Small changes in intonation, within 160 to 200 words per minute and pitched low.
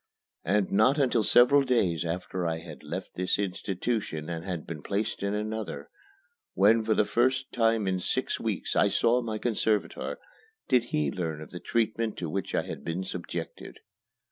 No: average, 4.7 semitones; average, 170 wpm; low, 100 Hz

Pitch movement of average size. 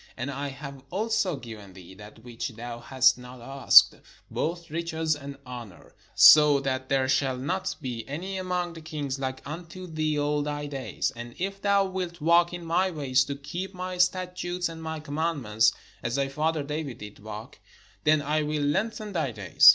Yes: average, 4.7 semitones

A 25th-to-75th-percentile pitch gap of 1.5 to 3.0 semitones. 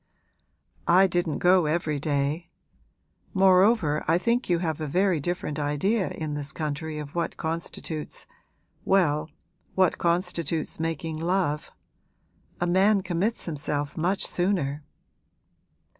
No: average, 3.4 semitones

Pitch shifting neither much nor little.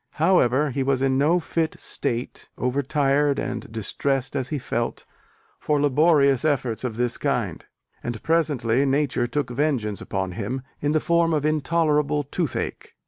Yes: average, 3.5 semitones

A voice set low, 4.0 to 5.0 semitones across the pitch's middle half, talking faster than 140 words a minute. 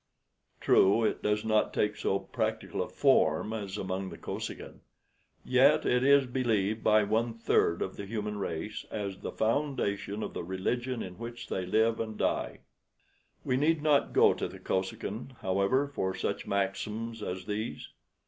No: low, 105 Hz; average, 3.2 semitones; average, 160 wpm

